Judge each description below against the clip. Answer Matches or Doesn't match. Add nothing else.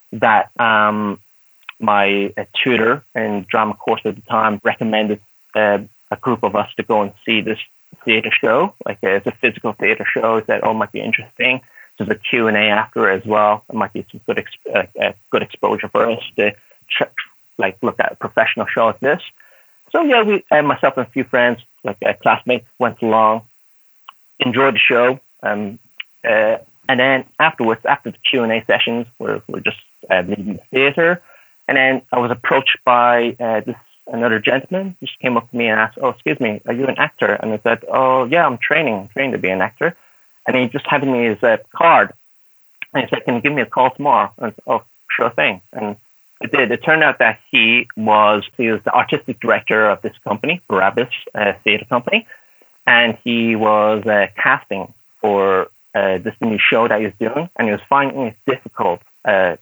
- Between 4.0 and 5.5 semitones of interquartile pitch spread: Doesn't match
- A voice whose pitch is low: Matches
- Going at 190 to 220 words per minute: Matches